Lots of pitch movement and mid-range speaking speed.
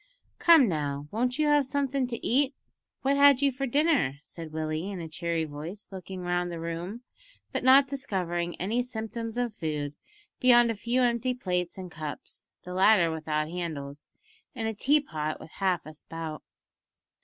Yes: wide, 7.4 semitones; average, 170 wpm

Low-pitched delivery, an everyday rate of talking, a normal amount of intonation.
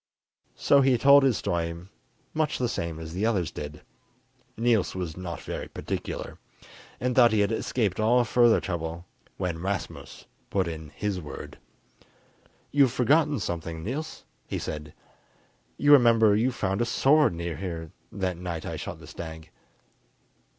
No: low, 100 Hz; average, 150 wpm; wide, 6.5 semitones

